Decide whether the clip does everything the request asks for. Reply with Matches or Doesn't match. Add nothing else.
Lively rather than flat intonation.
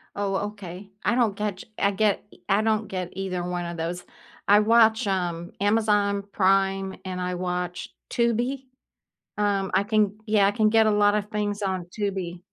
Doesn't match